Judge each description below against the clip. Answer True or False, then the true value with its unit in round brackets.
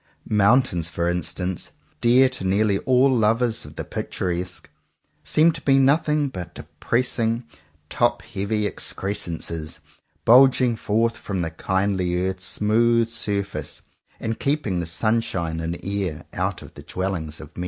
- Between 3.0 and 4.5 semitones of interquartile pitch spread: False (4.9 semitones)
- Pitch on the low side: True (105 Hz)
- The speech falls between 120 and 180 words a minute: True (145 wpm)